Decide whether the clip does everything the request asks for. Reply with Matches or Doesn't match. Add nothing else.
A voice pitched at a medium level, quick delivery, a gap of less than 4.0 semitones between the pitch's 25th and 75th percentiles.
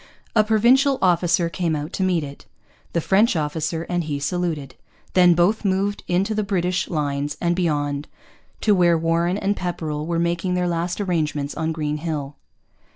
Doesn't match